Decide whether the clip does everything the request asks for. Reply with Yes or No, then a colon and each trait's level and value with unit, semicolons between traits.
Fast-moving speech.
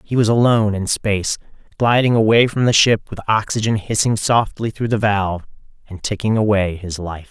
No: average, 180 wpm